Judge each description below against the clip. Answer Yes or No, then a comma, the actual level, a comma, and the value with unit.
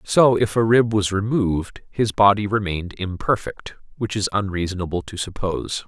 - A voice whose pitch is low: Yes, low, 100 Hz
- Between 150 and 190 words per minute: Yes, average, 155 wpm